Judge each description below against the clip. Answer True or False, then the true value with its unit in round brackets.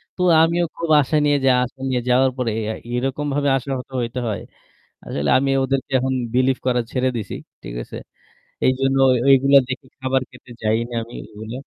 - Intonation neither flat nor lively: False (1.7 semitones)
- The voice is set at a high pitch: False (130 Hz)